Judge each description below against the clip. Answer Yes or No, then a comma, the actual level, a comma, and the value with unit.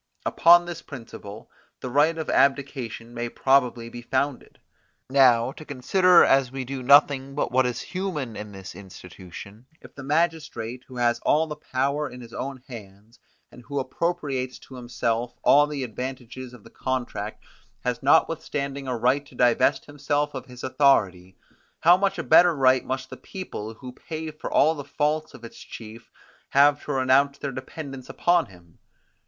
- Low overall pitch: Yes, low, 130 Hz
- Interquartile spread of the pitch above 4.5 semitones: No, average, 3.3 semitones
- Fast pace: No, average, 170 wpm